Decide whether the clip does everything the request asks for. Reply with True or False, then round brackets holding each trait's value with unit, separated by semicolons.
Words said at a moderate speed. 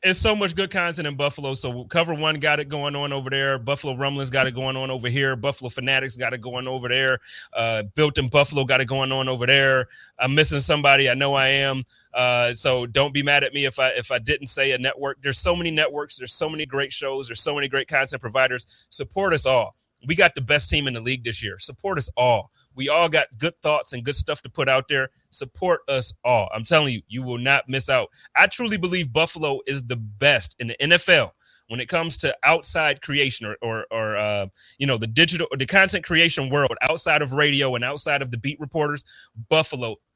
False (235 wpm)